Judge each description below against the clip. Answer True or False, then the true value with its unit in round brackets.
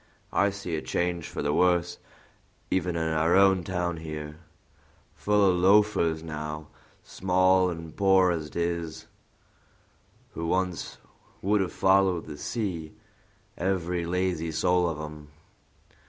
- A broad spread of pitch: False (2.6 semitones)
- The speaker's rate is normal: False (125 wpm)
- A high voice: False (90 Hz)